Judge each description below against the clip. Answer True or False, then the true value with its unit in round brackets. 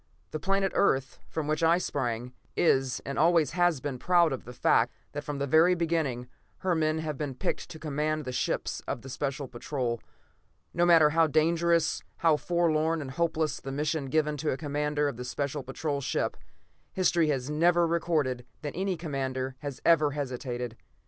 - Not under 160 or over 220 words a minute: True (180 wpm)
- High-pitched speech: False (150 Hz)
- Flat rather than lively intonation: False (3.6 semitones)